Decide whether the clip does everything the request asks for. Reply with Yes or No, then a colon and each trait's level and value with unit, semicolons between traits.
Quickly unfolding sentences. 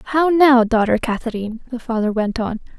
No: average, 170 wpm